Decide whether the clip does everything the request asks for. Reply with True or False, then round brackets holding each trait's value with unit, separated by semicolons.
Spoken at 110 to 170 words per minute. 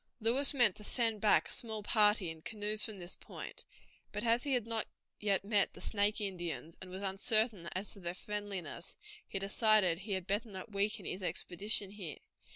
False (190 wpm)